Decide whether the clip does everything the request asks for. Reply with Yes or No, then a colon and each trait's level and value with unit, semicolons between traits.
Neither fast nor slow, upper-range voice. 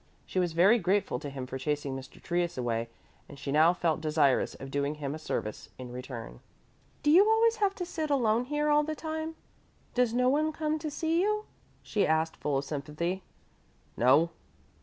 No: average, 190 wpm; medium, 175 Hz